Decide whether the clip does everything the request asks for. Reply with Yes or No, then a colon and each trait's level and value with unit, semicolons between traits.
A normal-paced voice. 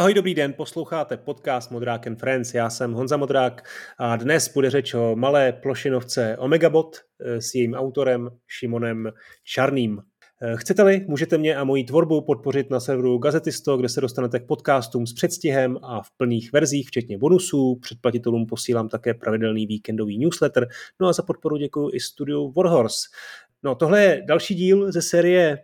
Yes: average, 160 wpm